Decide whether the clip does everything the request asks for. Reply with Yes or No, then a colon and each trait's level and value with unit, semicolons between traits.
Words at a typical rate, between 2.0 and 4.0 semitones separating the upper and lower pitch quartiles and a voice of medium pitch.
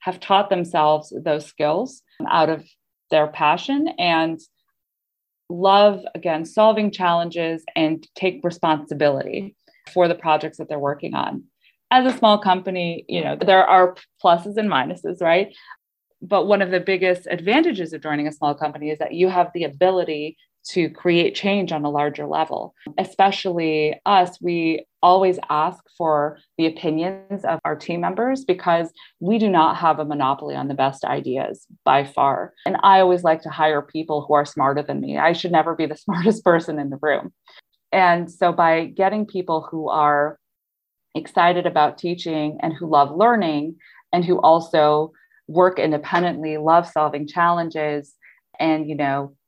Yes: average, 160 wpm; average, 3.4 semitones; medium, 170 Hz